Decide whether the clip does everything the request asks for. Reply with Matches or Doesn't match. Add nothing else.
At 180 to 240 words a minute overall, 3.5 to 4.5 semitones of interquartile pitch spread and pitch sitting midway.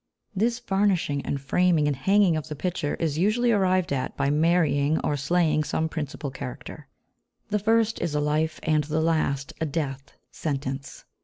Doesn't match